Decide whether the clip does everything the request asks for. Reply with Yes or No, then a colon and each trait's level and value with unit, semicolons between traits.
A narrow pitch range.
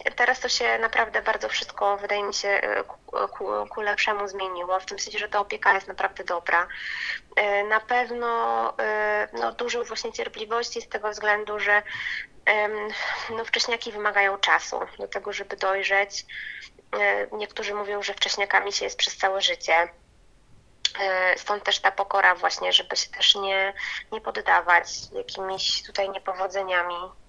Yes: narrow, 2.2 semitones